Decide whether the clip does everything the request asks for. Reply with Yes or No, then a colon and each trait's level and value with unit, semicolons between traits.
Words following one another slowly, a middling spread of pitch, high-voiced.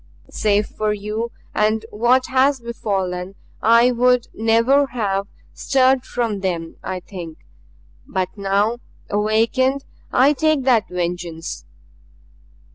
Yes: slow, 110 wpm; average, 4.3 semitones; high, 220 Hz